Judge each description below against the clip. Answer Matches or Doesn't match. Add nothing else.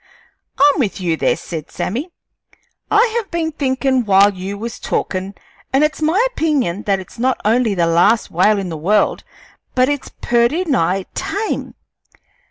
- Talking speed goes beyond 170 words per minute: Doesn't match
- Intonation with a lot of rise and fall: Matches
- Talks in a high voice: Matches